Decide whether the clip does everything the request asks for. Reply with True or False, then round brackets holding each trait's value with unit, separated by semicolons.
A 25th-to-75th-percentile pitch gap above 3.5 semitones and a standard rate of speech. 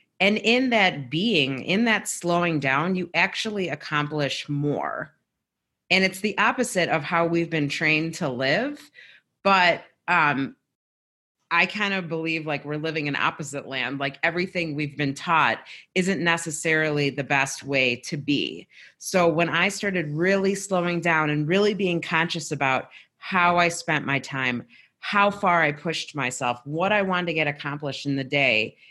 True (4.1 semitones; 160 wpm)